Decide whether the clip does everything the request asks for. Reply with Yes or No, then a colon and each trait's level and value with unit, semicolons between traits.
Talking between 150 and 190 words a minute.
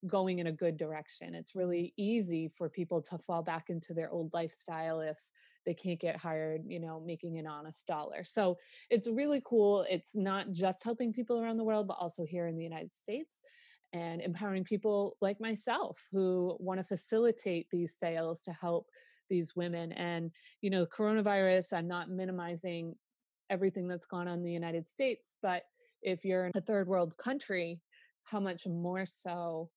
Yes: average, 180 wpm